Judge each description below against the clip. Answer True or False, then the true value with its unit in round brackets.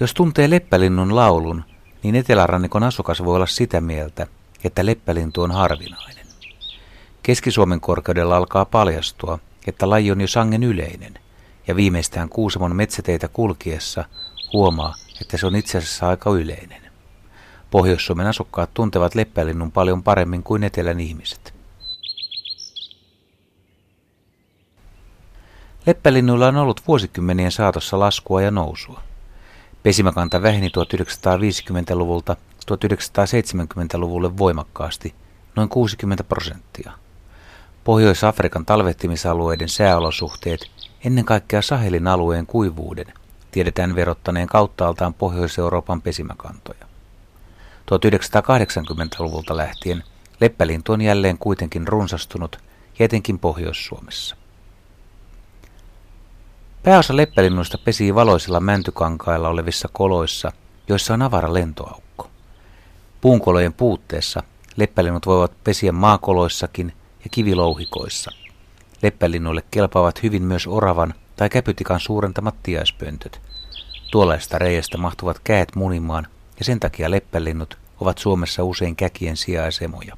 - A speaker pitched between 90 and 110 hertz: True (95 Hz)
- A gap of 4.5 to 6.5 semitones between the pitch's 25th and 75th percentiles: False (3.0 semitones)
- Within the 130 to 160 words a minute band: False (95 wpm)